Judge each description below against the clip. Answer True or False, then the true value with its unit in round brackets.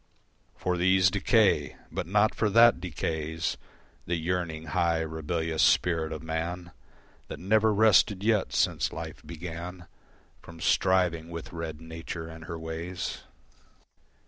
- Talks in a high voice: False (85 Hz)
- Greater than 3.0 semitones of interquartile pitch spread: False (2.4 semitones)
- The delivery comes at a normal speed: False (125 wpm)